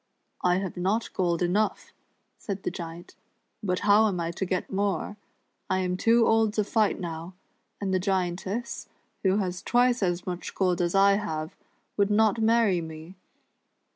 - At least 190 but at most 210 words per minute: No, average, 170 wpm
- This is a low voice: No, high, 190 Hz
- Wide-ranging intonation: No, average, 2.9 semitones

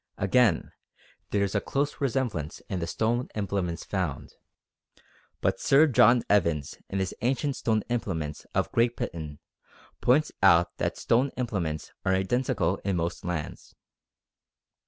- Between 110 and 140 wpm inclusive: Yes, slow, 135 wpm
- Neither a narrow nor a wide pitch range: No, wide, 6.2 semitones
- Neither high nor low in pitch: No, low, 100 Hz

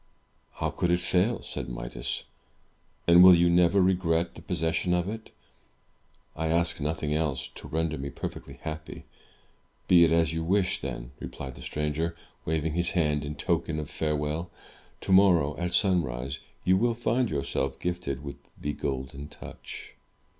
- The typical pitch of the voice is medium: No, very low, 80 Hz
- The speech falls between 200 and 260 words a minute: No, average, 155 wpm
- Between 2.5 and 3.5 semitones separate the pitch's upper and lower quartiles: Yes, average, 3.1 semitones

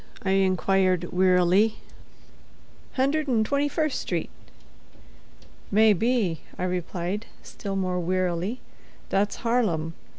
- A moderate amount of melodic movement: Yes, average, 3.8 semitones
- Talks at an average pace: No, slow, 100 wpm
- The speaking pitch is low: No, high, 195 Hz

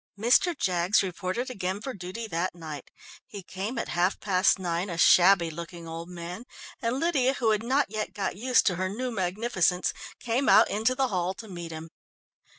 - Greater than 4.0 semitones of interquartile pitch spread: Yes, average, 4.8 semitones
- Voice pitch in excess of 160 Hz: Yes, high, 190 Hz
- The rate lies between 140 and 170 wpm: No, average, 185 wpm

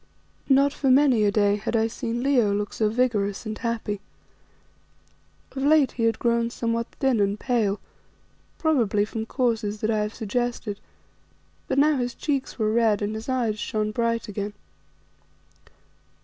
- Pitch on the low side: No, high, 230 Hz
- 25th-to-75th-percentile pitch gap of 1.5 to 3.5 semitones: Yes, average, 2.9 semitones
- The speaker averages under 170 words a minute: Yes, average, 155 wpm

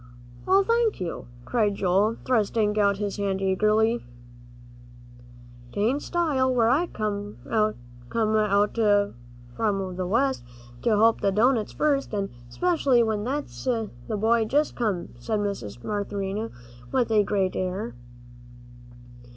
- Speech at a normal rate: No, slow, 115 wpm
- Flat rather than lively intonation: No, average, 3.2 semitones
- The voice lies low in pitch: No, high, 215 Hz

